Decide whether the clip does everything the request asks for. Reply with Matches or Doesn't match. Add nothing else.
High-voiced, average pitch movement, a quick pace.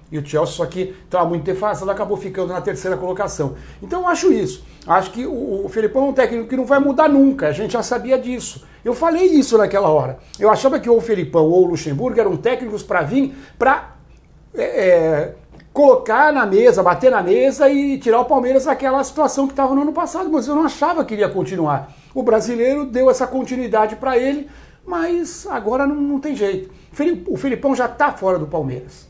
Doesn't match